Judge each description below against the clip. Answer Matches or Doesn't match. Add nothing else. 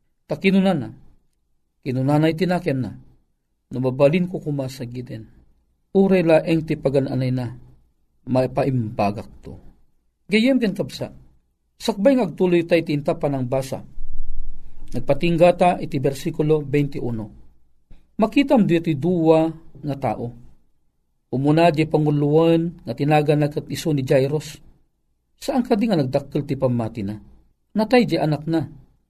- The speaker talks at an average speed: Matches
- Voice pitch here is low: Doesn't match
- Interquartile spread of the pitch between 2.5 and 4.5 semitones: Doesn't match